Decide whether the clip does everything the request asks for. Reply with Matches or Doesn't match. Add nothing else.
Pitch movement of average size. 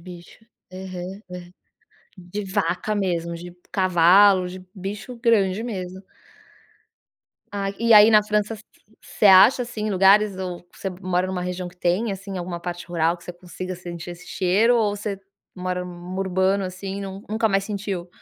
Doesn't match